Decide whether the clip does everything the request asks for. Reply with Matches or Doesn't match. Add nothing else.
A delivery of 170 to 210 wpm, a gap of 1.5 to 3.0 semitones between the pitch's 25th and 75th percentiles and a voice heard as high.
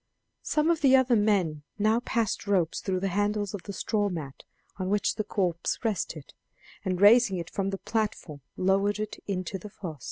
Matches